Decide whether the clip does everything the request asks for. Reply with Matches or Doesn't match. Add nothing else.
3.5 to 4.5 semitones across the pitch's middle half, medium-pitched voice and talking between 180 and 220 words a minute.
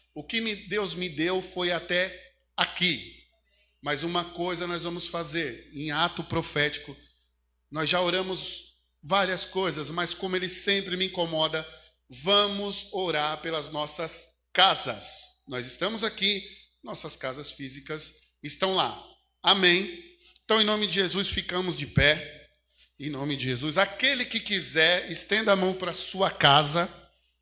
Doesn't match